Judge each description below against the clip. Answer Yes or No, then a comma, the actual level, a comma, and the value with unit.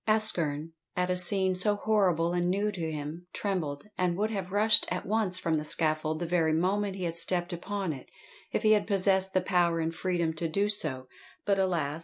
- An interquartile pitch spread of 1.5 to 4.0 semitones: Yes, average, 3.3 semitones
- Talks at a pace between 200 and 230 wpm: Yes, fast, 205 wpm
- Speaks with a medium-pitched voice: Yes, medium, 180 Hz